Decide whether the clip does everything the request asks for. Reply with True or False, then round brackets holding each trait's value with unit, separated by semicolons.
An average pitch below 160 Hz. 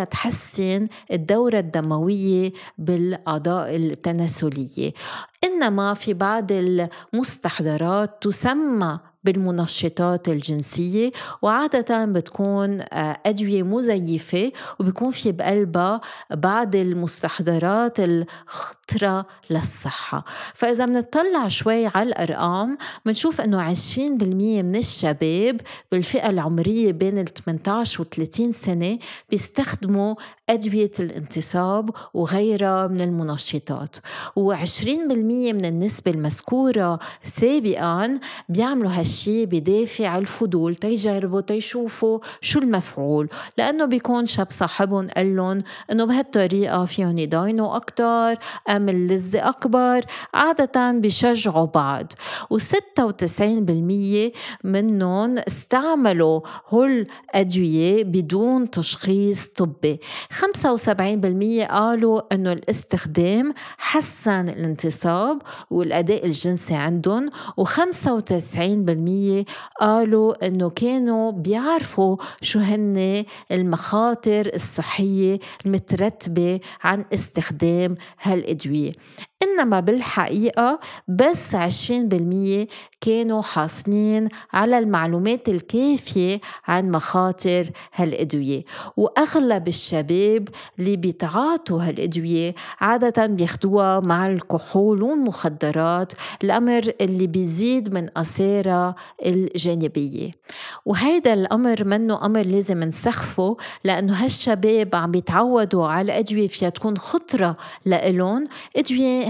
False (195 Hz)